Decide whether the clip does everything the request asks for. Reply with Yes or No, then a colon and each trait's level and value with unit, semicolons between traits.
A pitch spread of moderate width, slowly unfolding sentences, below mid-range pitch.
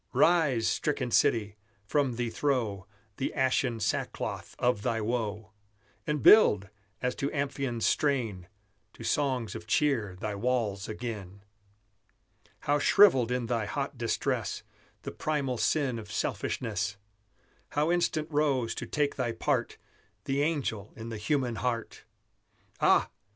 Yes: average, 4.5 semitones; slow, 130 wpm; low, 120 Hz